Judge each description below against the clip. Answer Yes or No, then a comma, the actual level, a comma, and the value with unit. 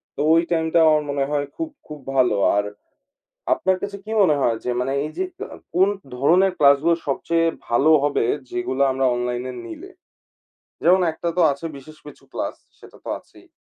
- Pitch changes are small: No, average, 4.2 semitones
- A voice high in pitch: No, medium, 150 Hz